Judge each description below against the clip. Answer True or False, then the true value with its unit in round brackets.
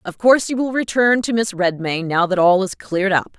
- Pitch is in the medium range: False (200 Hz)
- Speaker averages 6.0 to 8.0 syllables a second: False (5.5 syllables/s)